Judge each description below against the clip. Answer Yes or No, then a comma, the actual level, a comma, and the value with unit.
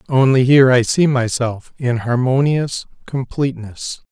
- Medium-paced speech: No, slow, 115 wpm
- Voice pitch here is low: Yes, low, 130 Hz